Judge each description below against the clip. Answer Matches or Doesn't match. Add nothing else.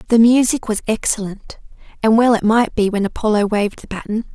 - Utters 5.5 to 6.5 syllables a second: Matches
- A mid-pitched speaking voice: Doesn't match